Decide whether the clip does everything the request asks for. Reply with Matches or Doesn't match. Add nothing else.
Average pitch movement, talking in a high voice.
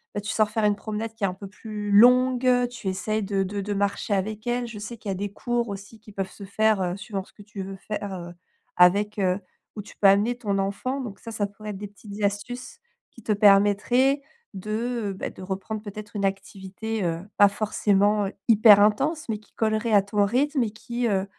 Doesn't match